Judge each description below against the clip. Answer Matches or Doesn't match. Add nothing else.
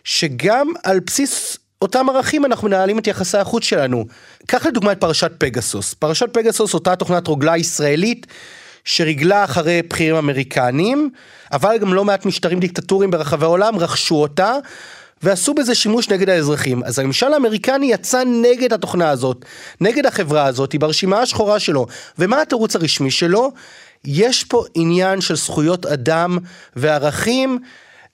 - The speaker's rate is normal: Matches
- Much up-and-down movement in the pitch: Matches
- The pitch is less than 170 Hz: Doesn't match